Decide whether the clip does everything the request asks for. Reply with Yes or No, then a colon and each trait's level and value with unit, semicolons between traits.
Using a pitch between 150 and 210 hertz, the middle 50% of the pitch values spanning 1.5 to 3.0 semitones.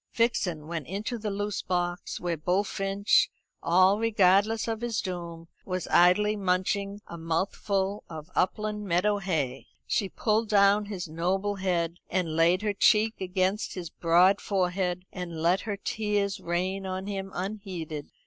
Yes: high, 190 Hz; narrow, 2.6 semitones